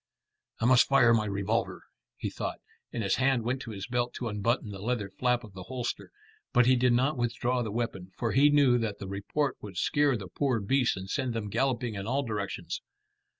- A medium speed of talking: No, fast, 210 wpm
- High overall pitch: No, low, 120 Hz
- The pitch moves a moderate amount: Yes, average, 3.6 semitones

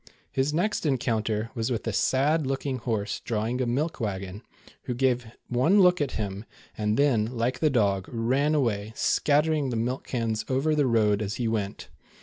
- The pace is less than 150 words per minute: No, average, 175 wpm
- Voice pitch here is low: Yes, low, 120 Hz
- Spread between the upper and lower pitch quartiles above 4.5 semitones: No, average, 4.0 semitones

